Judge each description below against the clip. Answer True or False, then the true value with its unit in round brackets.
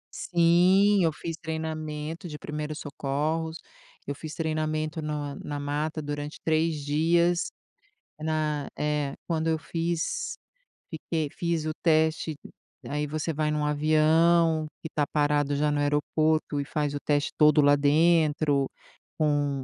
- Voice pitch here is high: False (155 Hz)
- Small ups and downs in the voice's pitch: True (1.6 semitones)